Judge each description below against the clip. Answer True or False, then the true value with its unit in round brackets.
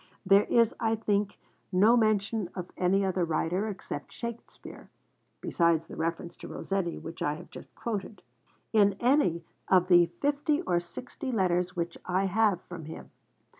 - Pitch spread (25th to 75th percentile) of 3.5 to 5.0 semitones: True (4.1 semitones)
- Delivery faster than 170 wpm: False (155 wpm)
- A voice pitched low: False (190 Hz)